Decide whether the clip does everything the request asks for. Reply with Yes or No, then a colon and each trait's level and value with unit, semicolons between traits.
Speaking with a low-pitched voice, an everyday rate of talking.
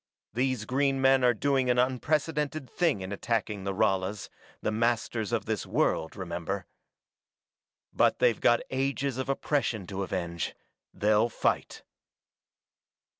No: low, 120 Hz; slow, 125 wpm